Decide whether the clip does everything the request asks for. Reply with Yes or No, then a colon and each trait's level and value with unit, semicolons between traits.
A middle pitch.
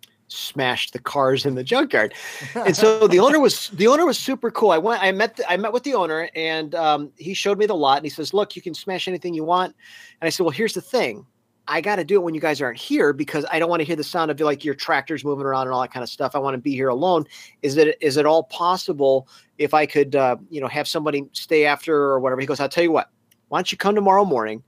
Yes: medium, 155 Hz